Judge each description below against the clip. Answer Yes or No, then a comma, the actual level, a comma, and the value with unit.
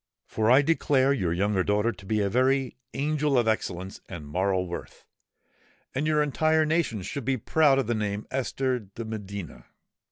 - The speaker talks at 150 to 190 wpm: Yes, average, 180 wpm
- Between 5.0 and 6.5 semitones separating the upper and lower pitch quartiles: Yes, wide, 5.6 semitones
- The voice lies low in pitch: Yes, low, 115 Hz